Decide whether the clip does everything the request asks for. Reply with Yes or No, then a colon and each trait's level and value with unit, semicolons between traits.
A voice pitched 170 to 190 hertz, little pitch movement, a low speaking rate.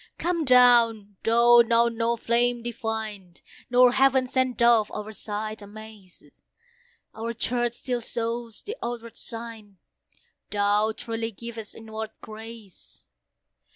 No: high, 230 Hz; narrow, 1.6 semitones; slow, 115 wpm